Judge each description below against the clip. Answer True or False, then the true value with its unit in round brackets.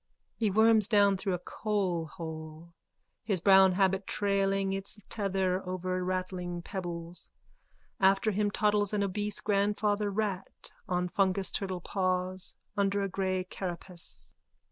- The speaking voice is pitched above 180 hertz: True (190 Hz)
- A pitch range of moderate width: False (1.9 semitones)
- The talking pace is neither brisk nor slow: False (120 wpm)